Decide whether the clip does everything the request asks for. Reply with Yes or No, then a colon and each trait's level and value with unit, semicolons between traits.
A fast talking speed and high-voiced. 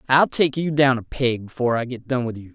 No: fast, 285 wpm; low, 125 Hz